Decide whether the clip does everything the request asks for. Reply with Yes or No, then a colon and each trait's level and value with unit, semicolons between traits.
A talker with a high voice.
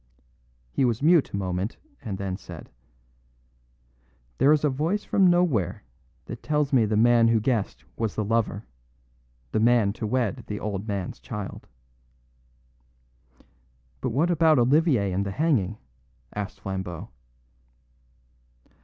No: low, 115 Hz